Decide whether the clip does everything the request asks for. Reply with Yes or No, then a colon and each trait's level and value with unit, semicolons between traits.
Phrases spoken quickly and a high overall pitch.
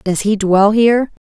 No: average, 190 wpm; high, 210 Hz